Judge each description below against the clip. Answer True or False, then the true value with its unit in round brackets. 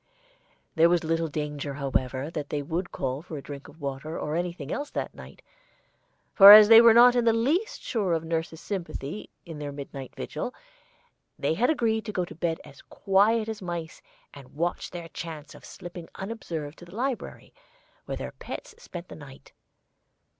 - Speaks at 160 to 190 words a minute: True (180 wpm)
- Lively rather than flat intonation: True (6.0 semitones)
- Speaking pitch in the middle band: True (170 Hz)